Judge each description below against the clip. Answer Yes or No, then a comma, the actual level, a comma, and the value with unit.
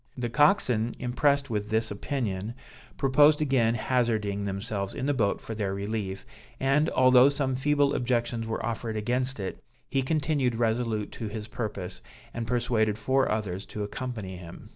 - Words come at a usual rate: Yes, average, 155 wpm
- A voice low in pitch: Yes, low, 115 Hz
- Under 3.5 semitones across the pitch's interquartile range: No, average, 3.9 semitones